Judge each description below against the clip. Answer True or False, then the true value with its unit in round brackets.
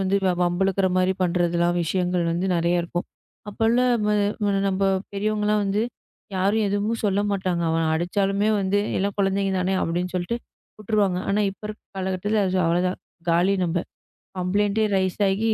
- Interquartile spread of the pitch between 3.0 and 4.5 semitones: False (2.5 semitones)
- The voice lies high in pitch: True (195 Hz)